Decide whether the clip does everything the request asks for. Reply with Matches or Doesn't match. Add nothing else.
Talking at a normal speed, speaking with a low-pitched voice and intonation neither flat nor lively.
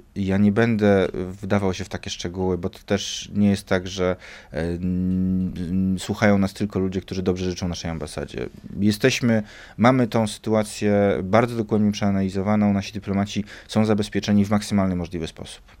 Doesn't match